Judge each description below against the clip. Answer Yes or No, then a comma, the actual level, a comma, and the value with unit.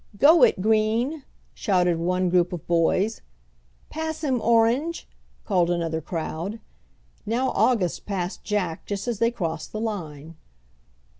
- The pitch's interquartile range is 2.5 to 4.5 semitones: No, average, 5.1 semitones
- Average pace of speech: No, slow, 130 wpm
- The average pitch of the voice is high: Yes, high, 200 Hz